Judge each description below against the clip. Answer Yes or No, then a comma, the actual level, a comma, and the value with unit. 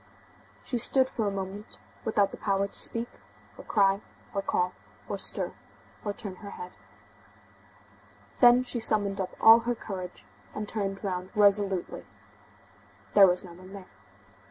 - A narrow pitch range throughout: Yes, narrow, 2.2 semitones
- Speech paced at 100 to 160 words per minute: Yes, average, 150 wpm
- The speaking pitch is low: No, high, 200 Hz